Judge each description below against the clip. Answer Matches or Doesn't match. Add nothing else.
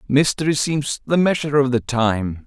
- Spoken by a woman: Doesn't match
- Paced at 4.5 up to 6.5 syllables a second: Matches